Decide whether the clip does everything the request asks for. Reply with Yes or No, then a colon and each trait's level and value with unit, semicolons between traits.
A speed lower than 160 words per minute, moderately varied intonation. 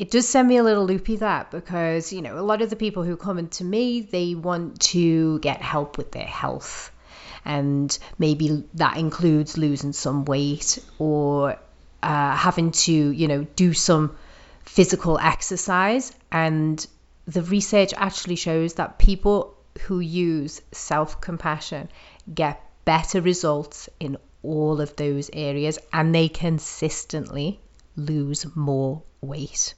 Yes: average, 140 wpm; average, 3.3 semitones